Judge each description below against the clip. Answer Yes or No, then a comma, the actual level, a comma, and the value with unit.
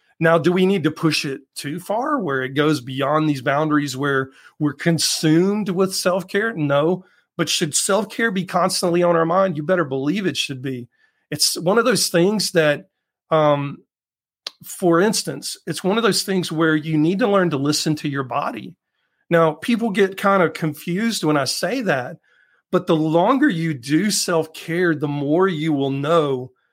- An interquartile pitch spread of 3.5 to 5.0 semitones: Yes, average, 3.9 semitones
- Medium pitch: Yes, medium, 165 Hz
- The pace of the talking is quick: No, average, 185 wpm